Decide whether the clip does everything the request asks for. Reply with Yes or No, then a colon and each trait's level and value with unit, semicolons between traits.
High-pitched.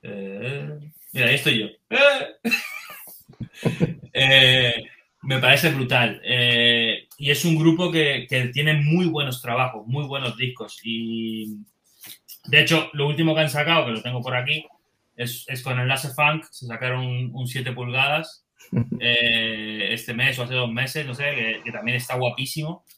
No: low, 130 Hz